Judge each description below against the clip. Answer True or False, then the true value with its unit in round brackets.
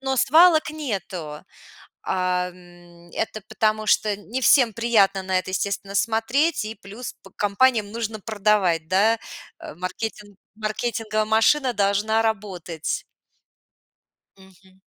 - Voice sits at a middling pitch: False (210 Hz)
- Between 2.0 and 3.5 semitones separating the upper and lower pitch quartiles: True (3.2 semitones)